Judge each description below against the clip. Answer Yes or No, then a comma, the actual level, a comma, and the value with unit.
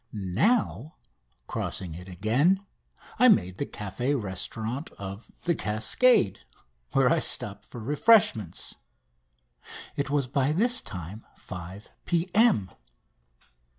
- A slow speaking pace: Yes, slow, 105 wpm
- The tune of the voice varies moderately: No, wide, 9.0 semitones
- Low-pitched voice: Yes, low, 115 Hz